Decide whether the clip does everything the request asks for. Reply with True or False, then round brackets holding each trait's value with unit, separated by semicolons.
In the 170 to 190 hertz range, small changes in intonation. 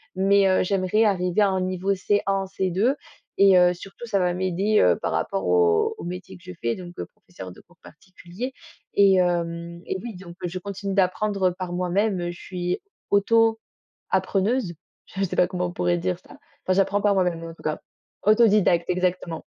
True (185 Hz; 2.1 semitones)